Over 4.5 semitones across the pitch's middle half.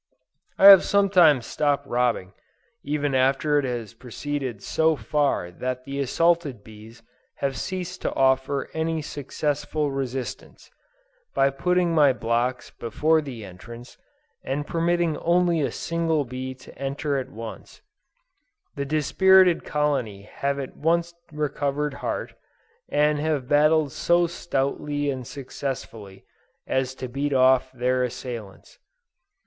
No: average, 3.4 semitones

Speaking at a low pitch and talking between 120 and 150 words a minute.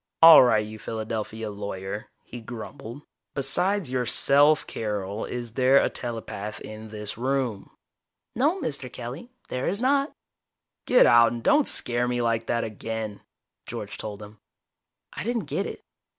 Yes: low, 120 Hz; average, 145 wpm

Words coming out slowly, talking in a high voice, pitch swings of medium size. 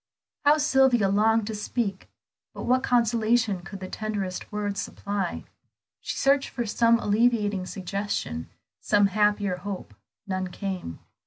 Yes: slow, 130 wpm; high, 205 Hz; average, 3.1 semitones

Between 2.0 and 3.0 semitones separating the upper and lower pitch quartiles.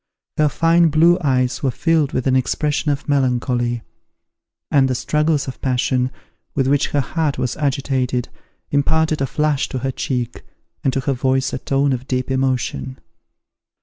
Yes: narrow, 2.5 semitones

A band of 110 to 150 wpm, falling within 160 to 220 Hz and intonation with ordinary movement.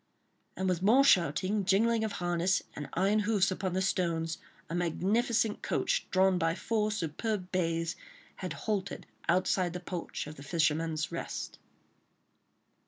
Yes: average, 140 wpm; medium, 185 Hz; average, 3.8 semitones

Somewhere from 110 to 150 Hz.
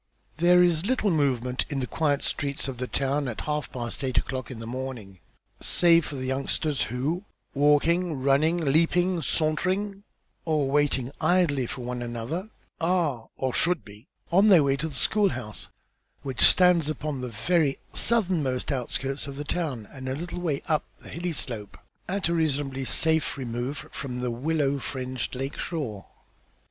Yes: medium, 140 Hz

